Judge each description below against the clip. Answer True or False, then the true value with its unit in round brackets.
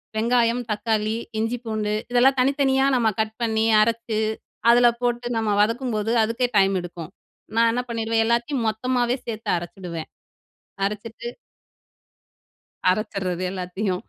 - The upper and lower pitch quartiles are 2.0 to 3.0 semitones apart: True (2.4 semitones)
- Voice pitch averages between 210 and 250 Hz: True (225 Hz)